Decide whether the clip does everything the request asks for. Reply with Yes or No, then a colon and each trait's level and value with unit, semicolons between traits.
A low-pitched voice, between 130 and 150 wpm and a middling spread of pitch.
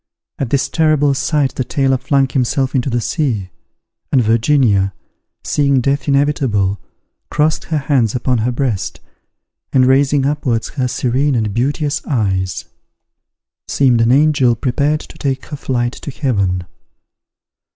Yes: low, 130 Hz; slow, 135 wpm; average, 3.3 semitones